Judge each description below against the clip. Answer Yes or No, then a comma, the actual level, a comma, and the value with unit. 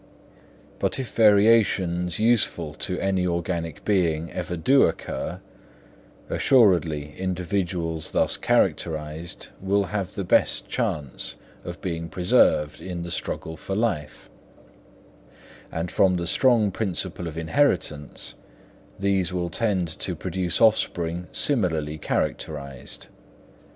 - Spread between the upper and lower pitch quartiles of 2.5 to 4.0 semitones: Yes, average, 3.2 semitones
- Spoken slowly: Yes, slow, 110 wpm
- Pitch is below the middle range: Yes, very low, 90 Hz